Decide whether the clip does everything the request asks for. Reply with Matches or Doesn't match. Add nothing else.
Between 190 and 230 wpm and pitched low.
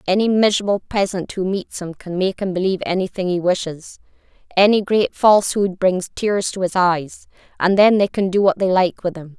Doesn't match